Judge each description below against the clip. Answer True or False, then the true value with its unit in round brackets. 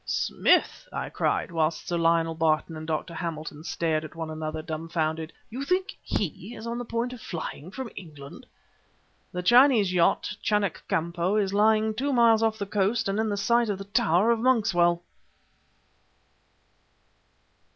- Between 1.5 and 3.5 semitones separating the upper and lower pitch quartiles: False (5.4 semitones)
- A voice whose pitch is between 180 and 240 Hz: True (190 Hz)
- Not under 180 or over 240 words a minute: False (160 wpm)